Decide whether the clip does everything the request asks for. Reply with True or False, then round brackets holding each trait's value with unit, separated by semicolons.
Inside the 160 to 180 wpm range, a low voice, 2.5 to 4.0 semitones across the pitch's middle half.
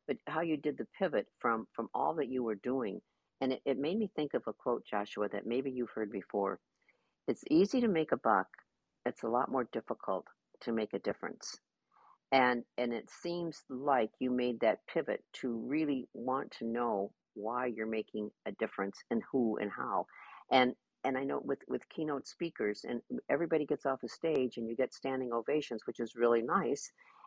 False (195 wpm; 125 Hz; 3.3 semitones)